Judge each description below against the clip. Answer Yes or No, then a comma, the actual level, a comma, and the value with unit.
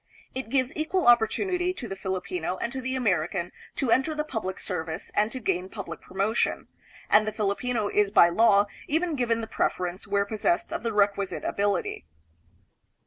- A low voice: No, high, 215 Hz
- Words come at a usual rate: Yes, average, 170 wpm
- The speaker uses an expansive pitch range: No, average, 4.8 semitones